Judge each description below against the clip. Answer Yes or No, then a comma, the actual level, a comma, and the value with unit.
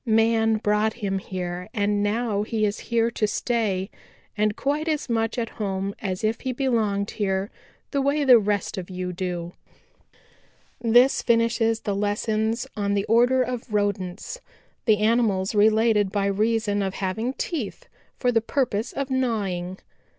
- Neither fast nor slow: Yes, average, 150 wpm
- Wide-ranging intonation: No, average, 2.8 semitones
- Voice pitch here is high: Yes, high, 215 Hz